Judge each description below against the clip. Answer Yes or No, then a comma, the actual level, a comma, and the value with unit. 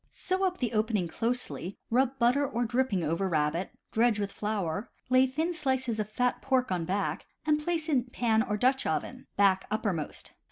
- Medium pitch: No, high, 235 Hz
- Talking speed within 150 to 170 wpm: No, average, 185 wpm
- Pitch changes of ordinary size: Yes, average, 4.7 semitones